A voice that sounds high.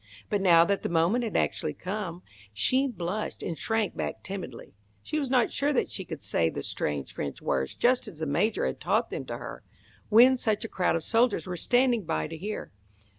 Yes: high, 195 Hz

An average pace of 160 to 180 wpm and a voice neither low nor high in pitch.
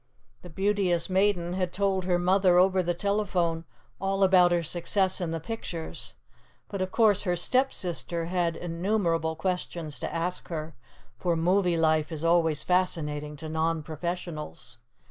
No: average, 145 wpm; medium, 175 Hz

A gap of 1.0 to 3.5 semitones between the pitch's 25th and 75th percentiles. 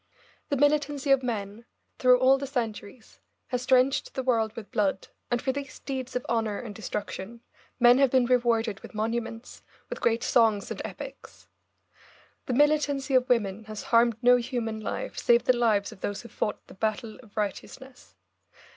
Yes: average, 3.0 semitones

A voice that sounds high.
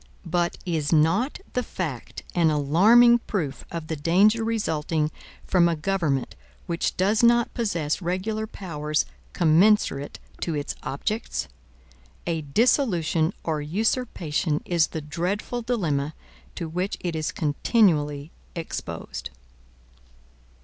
No: medium, 170 Hz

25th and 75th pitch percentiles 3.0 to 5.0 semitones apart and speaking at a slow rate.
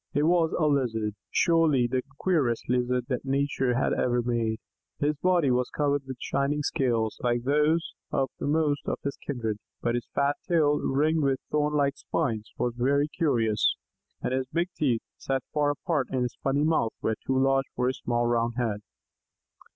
No: average, 3.4 semitones; average, 175 wpm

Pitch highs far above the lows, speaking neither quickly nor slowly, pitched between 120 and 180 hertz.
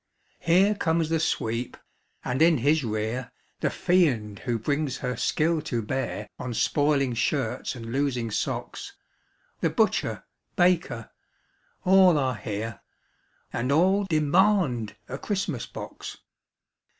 No: wide, 6.0 semitones; slow, 125 wpm; medium, 140 Hz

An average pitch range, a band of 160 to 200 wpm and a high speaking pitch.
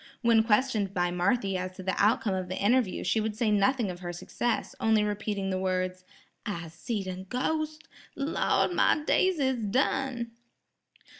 Yes: average, 4.7 semitones; average, 165 wpm; high, 210 Hz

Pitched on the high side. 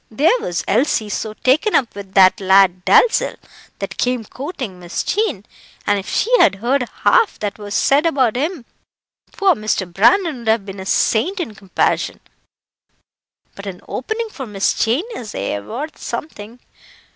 Yes: high, 225 Hz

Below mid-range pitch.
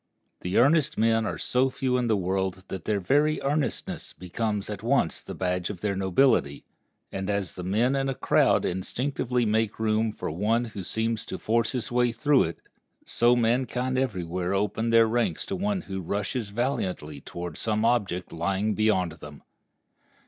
Yes: low, 110 Hz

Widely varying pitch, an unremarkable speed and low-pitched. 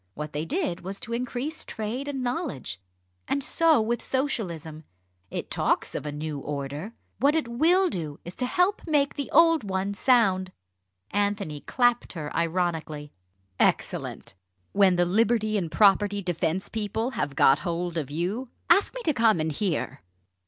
No: wide, 7.7 semitones; average, 160 wpm; high, 205 Hz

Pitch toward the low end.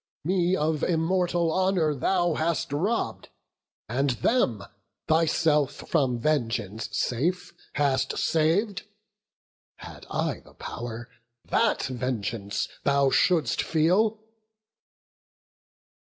No: medium, 155 Hz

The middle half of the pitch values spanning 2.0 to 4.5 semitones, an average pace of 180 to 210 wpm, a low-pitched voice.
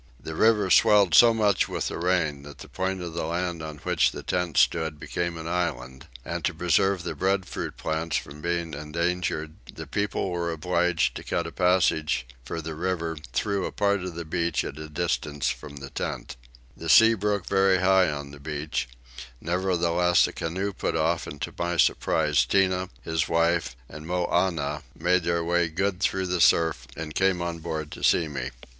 Yes: average, 2.8 semitones; average, 185 wpm; very low, 85 Hz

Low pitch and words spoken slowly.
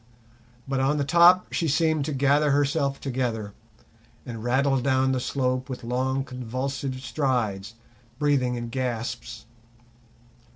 Yes: low, 130 Hz; slow, 125 wpm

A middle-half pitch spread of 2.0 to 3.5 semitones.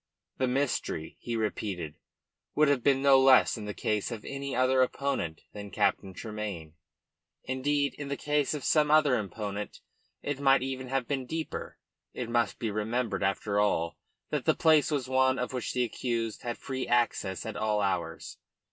No: average, 4.4 semitones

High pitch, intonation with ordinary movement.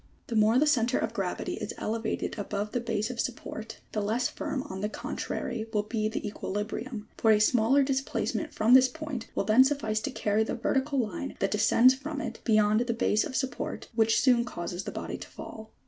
Yes: high, 225 Hz; average, 3.0 semitones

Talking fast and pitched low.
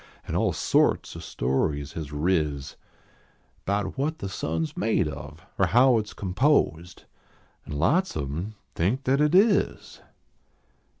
No: average, 145 wpm; very low, 95 Hz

